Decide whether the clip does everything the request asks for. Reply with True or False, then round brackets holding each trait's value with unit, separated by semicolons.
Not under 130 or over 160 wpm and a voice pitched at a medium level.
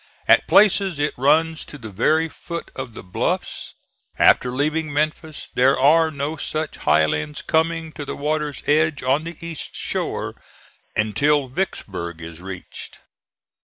True (140 wpm; 145 Hz)